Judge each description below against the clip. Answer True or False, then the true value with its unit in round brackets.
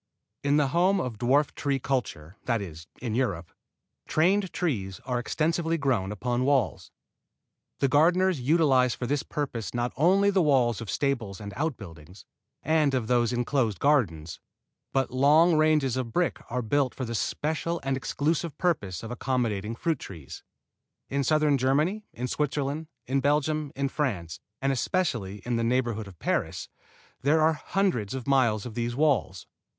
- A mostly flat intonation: False (4.9 semitones)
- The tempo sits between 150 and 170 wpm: True (155 wpm)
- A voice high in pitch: False (130 Hz)